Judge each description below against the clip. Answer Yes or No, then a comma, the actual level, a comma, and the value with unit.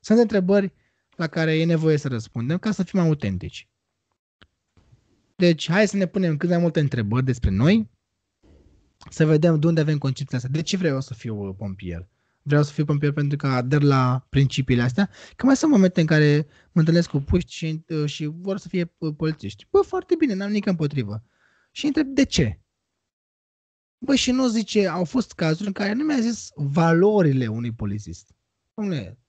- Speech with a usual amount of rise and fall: No, wide, 7.1 semitones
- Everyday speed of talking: No, fast, 180 wpm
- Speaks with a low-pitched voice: No, medium, 160 Hz